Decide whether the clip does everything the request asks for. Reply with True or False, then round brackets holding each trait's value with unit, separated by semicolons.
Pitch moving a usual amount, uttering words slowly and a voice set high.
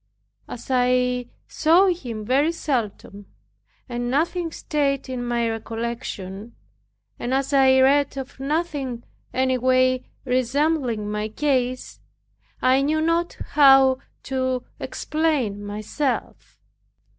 True (3.1 semitones; 105 wpm; 260 Hz)